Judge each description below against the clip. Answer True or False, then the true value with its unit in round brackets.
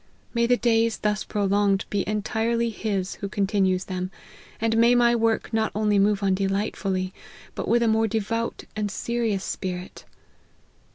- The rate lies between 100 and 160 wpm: True (155 wpm)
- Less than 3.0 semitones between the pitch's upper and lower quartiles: True (2.6 semitones)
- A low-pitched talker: False (210 Hz)